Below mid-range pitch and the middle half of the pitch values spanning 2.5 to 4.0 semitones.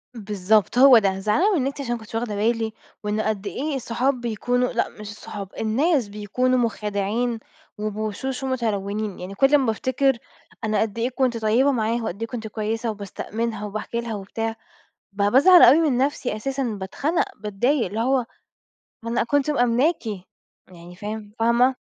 No: high, 230 Hz; average, 3.4 semitones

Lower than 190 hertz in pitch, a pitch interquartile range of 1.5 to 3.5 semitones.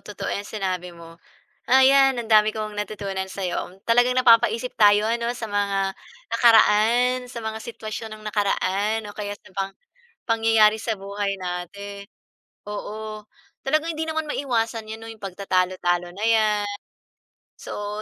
No: high, 215 Hz; narrow, 2.4 semitones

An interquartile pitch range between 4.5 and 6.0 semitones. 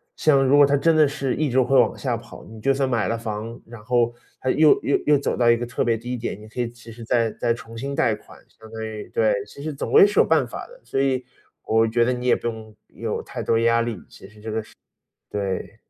No: average, 3.3 semitones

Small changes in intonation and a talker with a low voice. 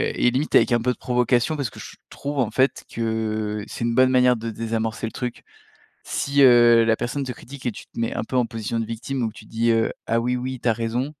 Yes: narrow, 2.0 semitones; low, 120 Hz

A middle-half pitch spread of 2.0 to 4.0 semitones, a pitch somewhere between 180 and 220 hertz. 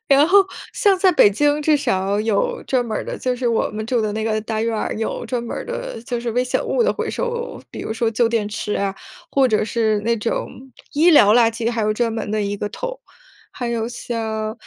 No: average, 3.4 semitones; high, 230 Hz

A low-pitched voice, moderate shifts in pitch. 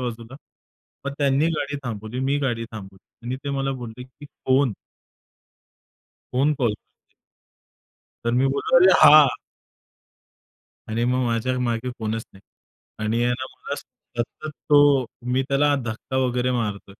Yes: low, 125 Hz; average, 3.2 semitones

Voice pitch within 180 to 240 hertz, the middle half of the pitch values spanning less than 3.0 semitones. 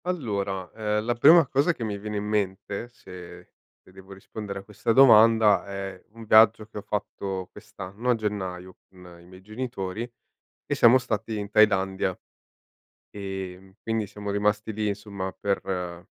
No: low, 105 Hz; narrow, 2.4 semitones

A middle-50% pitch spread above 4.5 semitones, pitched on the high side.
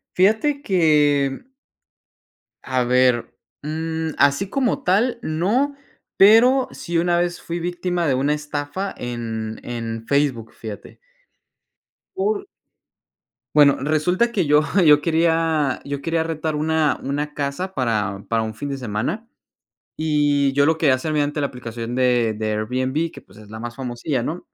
No: average, 5.2 semitones; medium, 150 Hz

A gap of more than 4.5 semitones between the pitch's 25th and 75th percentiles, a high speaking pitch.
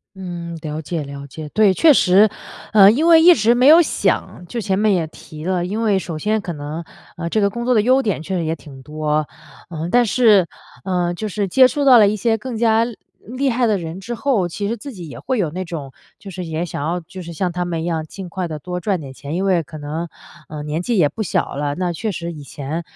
No: average, 5.3 semitones; medium, 180 Hz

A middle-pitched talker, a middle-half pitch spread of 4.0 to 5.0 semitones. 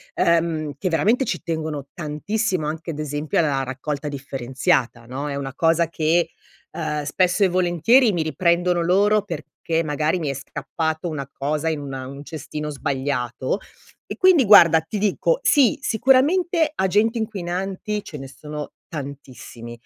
Yes: medium, 160 Hz; average, 4.7 semitones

